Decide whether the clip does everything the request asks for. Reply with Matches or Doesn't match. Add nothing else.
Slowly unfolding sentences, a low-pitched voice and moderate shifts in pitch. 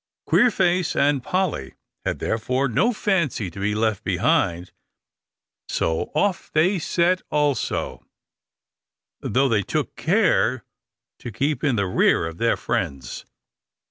Doesn't match